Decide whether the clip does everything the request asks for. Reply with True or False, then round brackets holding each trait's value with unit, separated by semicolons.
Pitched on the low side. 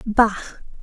False (215 Hz)